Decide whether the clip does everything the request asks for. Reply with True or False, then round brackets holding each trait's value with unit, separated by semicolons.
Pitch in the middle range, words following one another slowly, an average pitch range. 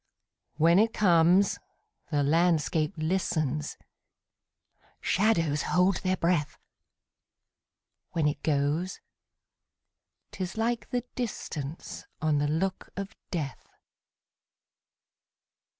True (170 Hz; 75 wpm; 4.0 semitones)